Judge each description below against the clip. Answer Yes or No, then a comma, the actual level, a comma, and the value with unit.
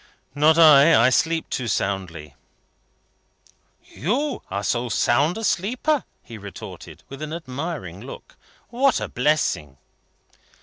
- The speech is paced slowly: Yes, slow, 120 wpm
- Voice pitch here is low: No, medium, 145 Hz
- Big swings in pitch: Yes, wide, 7.6 semitones